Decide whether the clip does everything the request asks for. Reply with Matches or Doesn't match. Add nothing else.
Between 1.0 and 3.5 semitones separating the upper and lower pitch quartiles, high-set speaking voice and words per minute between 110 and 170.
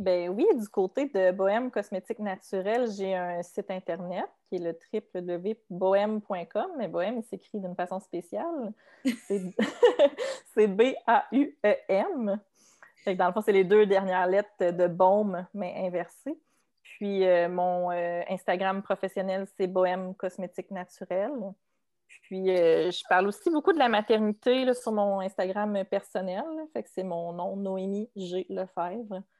Matches